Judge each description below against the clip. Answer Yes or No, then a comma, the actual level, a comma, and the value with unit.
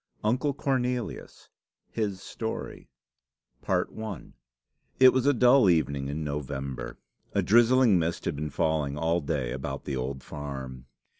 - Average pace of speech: No, slow, 125 wpm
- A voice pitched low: Yes, very low, 80 Hz